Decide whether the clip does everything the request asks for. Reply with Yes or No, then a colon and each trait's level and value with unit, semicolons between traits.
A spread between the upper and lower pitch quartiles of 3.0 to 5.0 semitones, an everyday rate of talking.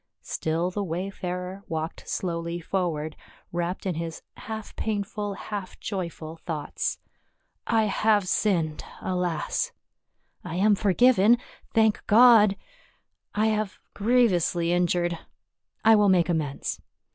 No: average, 3.7 semitones; slow, 120 wpm